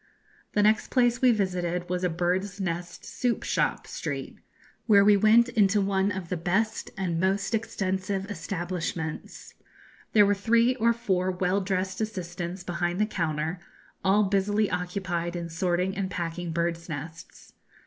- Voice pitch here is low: No, high, 190 Hz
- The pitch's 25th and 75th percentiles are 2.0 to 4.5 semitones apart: Yes, average, 2.8 semitones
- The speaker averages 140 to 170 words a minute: Yes, average, 150 wpm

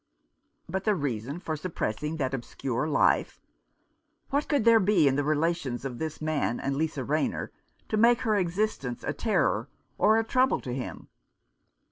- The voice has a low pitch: No, medium, 155 Hz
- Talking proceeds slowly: No, average, 160 wpm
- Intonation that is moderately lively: No, wide, 7.4 semitones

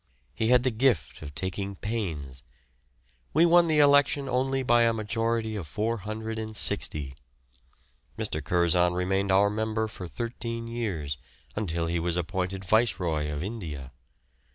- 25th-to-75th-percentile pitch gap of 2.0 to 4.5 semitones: No, average, 5.1 semitones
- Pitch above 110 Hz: No, low, 105 Hz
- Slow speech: Yes, slow, 130 wpm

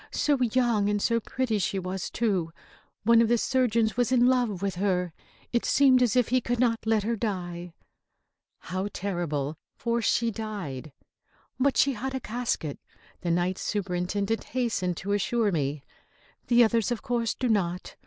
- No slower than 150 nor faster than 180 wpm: Yes, average, 165 wpm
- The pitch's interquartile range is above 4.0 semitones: Yes, average, 4.7 semitones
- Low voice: No, high, 215 Hz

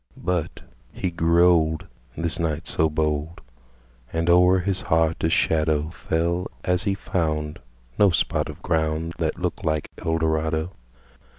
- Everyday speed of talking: No, slow, 120 wpm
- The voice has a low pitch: Yes, very low, 80 Hz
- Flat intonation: Yes, narrow, 1.9 semitones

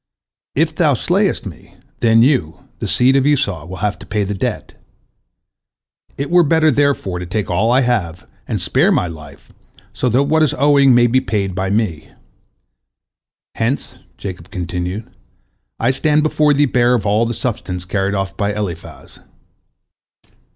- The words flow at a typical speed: Yes, average, 160 wpm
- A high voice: No, low, 115 Hz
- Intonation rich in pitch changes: Yes, wide, 6.4 semitones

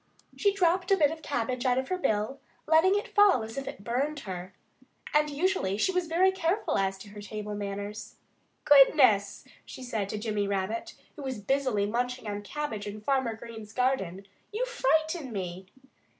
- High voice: Yes, high, 245 Hz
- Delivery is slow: No, average, 175 wpm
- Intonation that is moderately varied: No, wide, 7.2 semitones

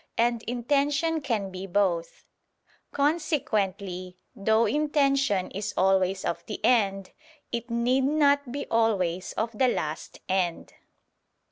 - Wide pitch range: Yes, wide, 6.3 semitones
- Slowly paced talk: Yes, slow, 115 wpm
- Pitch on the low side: No, high, 225 Hz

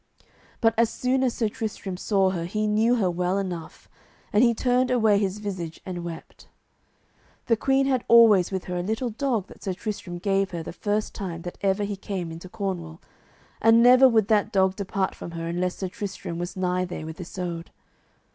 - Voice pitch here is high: Yes, high, 195 Hz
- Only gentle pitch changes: No, average, 3.8 semitones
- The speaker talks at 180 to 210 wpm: Yes, average, 195 wpm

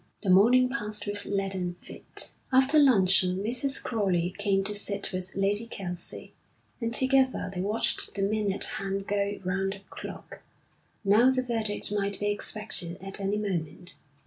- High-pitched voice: Yes, high, 200 Hz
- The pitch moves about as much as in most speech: No, narrow, 2.3 semitones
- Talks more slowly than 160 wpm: Yes, average, 150 wpm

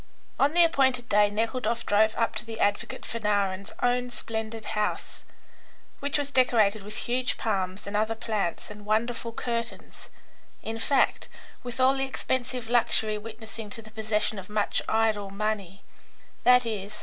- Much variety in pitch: No, average, 2.7 semitones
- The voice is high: Yes, high, 220 Hz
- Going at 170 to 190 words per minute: No, average, 150 wpm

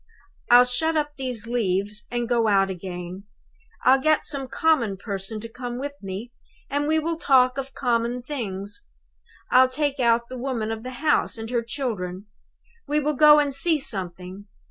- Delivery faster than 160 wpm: Yes, average, 170 wpm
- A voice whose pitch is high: Yes, high, 245 Hz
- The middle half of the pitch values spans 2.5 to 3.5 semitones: No, average, 5.0 semitones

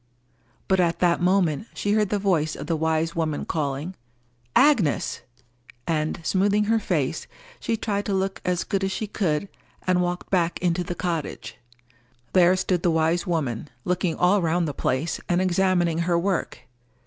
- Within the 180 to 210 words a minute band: No, average, 165 wpm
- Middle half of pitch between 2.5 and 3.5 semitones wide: Yes, average, 2.9 semitones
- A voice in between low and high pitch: Yes, medium, 175 Hz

